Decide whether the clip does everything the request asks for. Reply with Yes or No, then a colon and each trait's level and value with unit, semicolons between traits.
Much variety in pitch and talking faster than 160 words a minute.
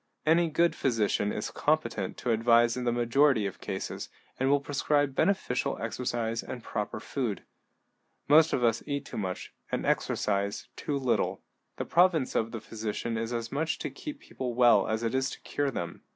No: average, 4.0 semitones; average, 180 wpm